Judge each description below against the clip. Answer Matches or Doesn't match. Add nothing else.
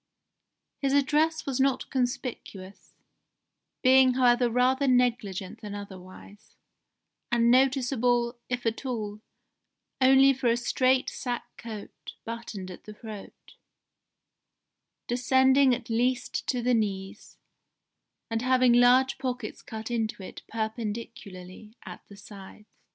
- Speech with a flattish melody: Doesn't match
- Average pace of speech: Doesn't match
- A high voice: Matches